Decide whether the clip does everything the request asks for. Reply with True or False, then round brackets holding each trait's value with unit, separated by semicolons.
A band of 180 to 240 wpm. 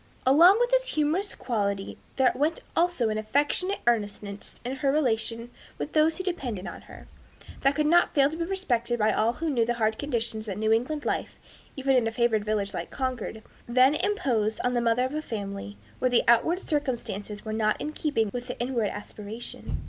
True (195 wpm)